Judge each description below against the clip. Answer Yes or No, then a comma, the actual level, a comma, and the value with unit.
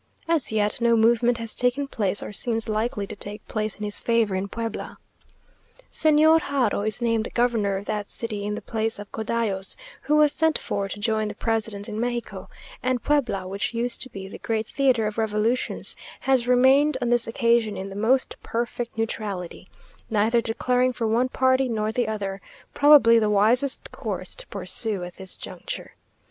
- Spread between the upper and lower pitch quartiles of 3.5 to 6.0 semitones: No, average, 2.9 semitones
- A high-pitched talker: Yes, high, 225 Hz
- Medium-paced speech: Yes, average, 180 wpm